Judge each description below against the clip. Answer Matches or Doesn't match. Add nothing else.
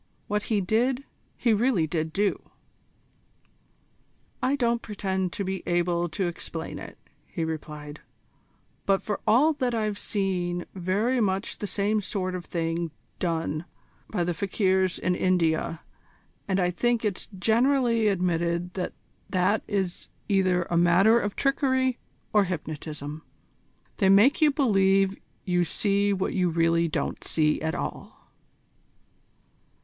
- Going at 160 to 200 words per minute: Doesn't match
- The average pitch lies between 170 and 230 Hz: Matches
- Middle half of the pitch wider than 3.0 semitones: Matches